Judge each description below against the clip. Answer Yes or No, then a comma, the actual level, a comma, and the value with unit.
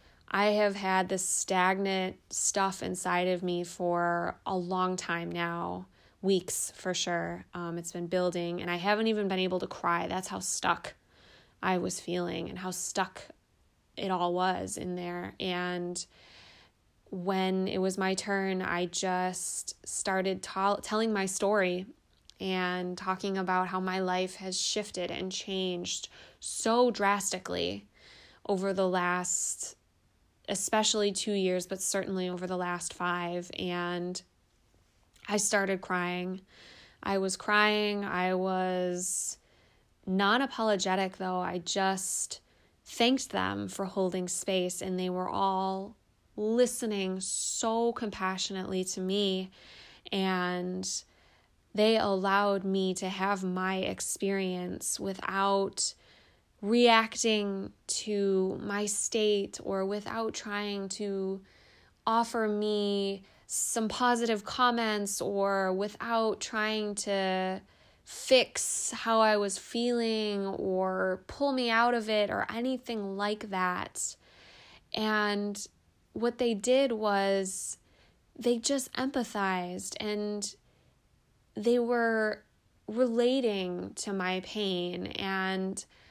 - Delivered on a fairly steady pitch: Yes, narrow, 2.2 semitones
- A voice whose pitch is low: No, high, 190 Hz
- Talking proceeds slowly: Yes, slow, 115 wpm